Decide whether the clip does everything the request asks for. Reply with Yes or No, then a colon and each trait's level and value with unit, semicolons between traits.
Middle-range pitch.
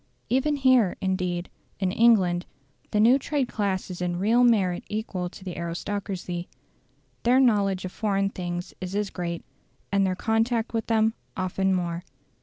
No: high, 195 Hz